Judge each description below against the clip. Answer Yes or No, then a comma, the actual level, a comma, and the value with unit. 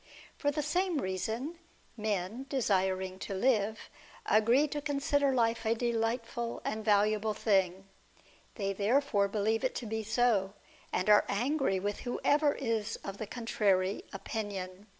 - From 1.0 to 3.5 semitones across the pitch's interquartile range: No, average, 3.9 semitones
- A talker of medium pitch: No, high, 220 Hz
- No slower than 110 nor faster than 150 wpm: Yes, average, 140 wpm